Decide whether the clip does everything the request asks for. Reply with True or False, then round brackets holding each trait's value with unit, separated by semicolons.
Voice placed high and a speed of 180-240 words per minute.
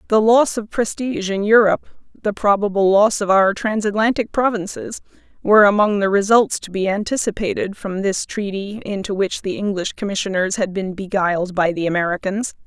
False (200 Hz; 165 wpm)